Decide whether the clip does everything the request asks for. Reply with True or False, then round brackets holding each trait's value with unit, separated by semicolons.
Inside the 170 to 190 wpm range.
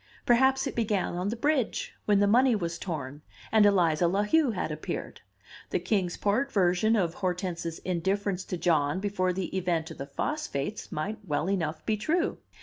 True (175 wpm)